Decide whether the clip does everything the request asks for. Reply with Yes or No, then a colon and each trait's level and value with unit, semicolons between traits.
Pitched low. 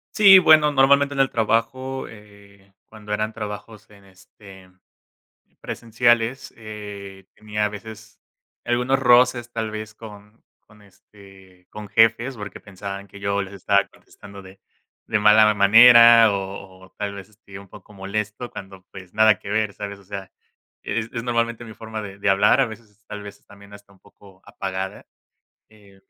Yes: low, 105 Hz